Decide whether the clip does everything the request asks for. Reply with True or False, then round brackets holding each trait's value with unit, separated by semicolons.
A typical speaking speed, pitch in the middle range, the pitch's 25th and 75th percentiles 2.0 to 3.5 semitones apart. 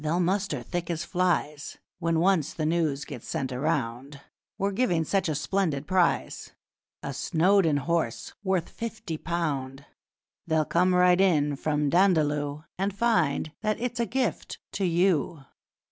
False (145 wpm; 165 Hz; 4.2 semitones)